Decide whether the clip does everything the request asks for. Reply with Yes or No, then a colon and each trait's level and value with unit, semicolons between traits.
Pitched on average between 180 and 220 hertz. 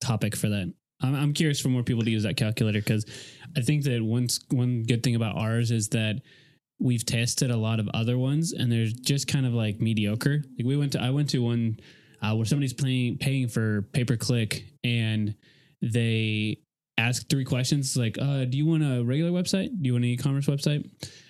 No: low, 125 Hz